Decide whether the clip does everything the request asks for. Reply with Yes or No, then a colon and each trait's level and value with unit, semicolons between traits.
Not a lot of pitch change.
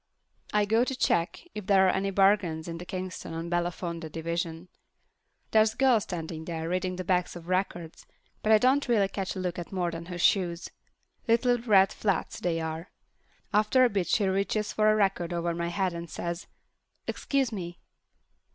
No: average, 3.6 semitones